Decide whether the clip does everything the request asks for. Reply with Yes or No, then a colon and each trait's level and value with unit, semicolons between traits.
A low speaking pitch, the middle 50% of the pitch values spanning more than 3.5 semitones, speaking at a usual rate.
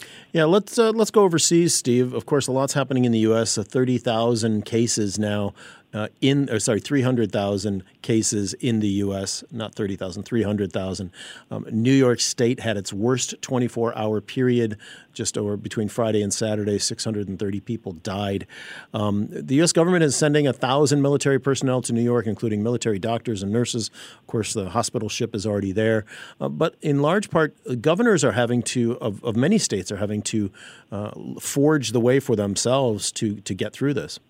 Yes: low, 115 Hz; average, 4.0 semitones; average, 180 wpm